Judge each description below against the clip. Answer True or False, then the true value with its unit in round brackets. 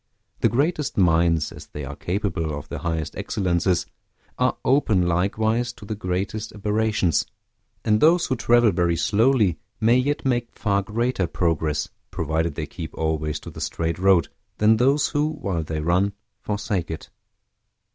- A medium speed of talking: True (155 wpm)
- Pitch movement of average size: False (5.9 semitones)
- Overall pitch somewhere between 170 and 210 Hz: False (100 Hz)